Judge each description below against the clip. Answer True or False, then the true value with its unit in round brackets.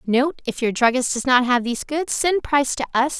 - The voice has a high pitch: True (265 Hz)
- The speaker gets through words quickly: True (225 wpm)